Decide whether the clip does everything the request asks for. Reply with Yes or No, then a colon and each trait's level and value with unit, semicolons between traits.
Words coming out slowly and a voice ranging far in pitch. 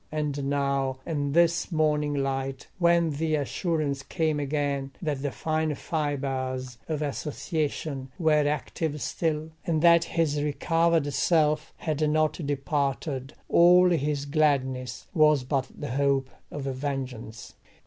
No: slow, 125 wpm; narrow, 2.4 semitones